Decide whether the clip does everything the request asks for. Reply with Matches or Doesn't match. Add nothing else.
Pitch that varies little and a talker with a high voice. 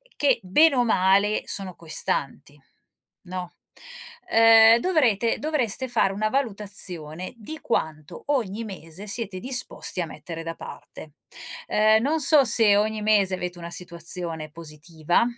Doesn't match